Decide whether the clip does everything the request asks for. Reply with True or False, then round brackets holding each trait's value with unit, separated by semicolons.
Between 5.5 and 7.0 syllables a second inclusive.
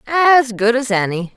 False (4.1 syllables/s)